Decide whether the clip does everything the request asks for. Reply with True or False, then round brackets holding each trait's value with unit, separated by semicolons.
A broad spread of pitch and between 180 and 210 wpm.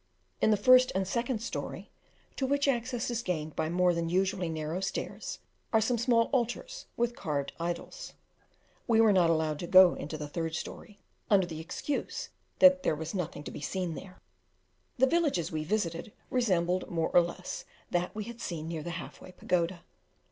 True (6.0 semitones; 185 wpm)